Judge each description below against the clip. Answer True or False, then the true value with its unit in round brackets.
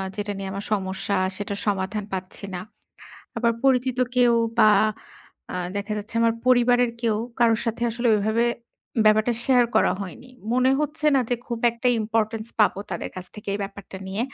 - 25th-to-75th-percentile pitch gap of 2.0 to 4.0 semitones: True (3.2 semitones)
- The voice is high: True (220 Hz)